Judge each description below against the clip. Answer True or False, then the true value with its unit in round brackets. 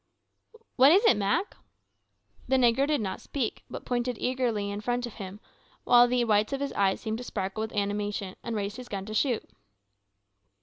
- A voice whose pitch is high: True (225 Hz)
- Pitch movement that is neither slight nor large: True (3.5 semitones)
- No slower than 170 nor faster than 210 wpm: True (180 wpm)